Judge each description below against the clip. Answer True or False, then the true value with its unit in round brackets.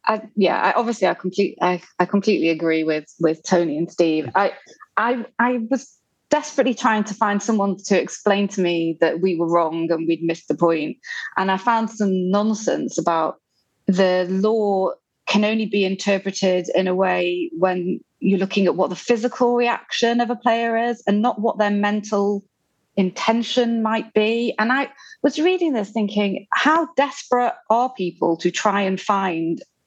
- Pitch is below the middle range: False (205 Hz)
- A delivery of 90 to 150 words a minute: False (175 wpm)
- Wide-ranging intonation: False (4.3 semitones)